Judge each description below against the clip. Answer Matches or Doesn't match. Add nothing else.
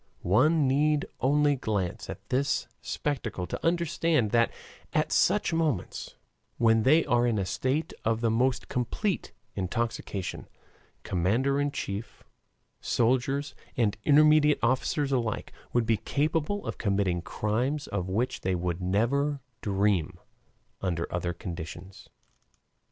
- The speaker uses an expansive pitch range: Matches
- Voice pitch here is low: Matches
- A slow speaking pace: Matches